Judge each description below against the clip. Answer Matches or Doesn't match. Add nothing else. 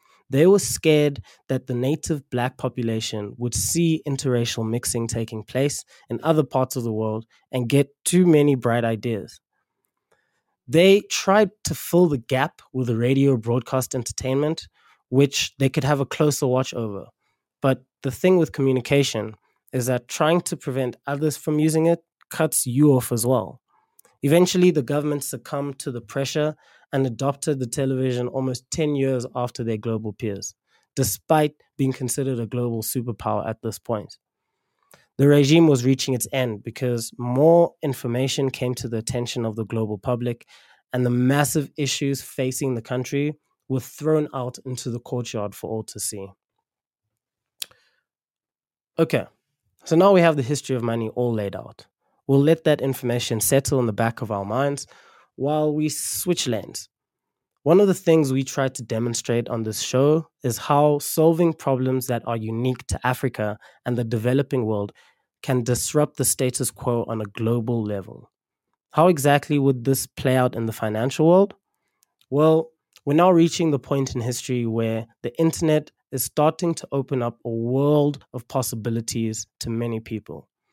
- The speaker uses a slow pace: Doesn't match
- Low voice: Matches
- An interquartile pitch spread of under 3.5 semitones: Doesn't match